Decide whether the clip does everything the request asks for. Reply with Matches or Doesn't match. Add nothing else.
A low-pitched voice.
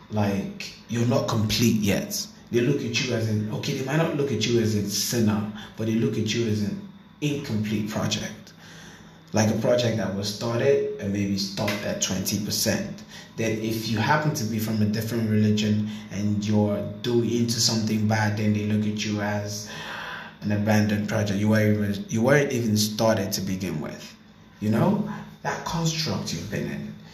Matches